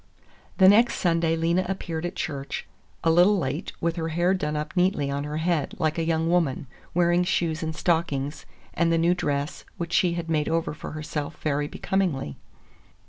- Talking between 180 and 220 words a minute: Yes, average, 185 wpm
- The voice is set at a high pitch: No, medium, 165 Hz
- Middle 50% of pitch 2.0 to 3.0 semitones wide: Yes, narrow, 2.5 semitones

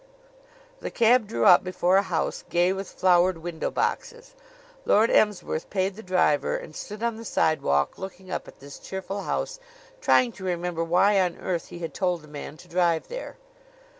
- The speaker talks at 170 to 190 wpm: Yes, average, 180 wpm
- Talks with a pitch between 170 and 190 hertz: Yes, medium, 185 Hz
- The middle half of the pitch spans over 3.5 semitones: No, average, 3.2 semitones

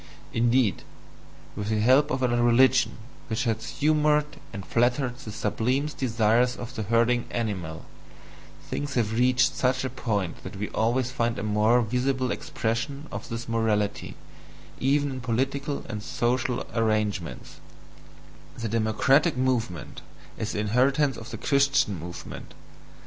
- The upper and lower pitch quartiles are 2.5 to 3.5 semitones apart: Yes, average, 3.1 semitones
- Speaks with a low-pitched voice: Yes, low, 120 Hz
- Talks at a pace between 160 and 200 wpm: No, slow, 135 wpm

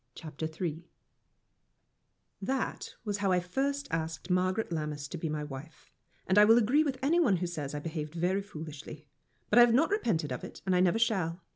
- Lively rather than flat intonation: Yes, wide, 5.8 semitones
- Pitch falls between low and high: Yes, medium, 180 Hz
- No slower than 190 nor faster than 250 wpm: Yes, average, 195 wpm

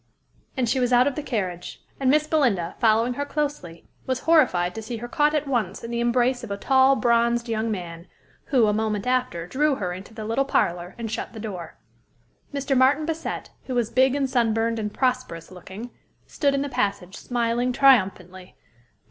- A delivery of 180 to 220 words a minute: Yes, average, 190 wpm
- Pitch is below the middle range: No, high, 235 Hz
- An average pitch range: Yes, average, 4.3 semitones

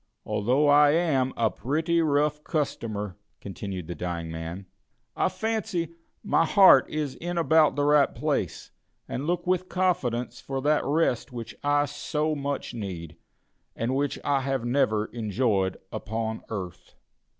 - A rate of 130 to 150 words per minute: Yes, average, 140 wpm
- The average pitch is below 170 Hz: Yes, low, 135 Hz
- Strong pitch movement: Yes, wide, 5.9 semitones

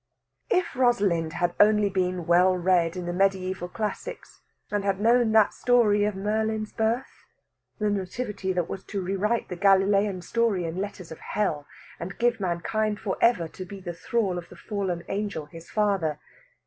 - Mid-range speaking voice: No, high, 195 Hz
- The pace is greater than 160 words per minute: Yes, average, 170 wpm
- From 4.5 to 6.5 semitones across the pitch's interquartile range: No, average, 3.0 semitones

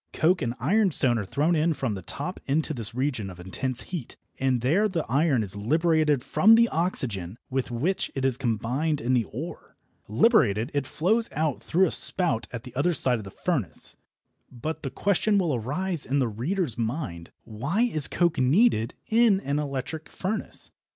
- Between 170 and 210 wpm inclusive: Yes, average, 175 wpm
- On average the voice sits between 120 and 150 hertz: Yes, medium, 140 Hz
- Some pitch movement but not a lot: No, wide, 6.4 semitones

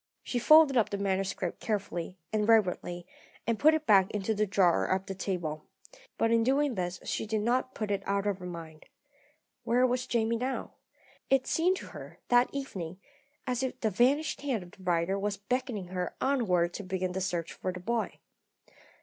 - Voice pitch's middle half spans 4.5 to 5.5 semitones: Yes, average, 5.1 semitones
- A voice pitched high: Yes, high, 205 Hz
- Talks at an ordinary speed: Yes, average, 190 wpm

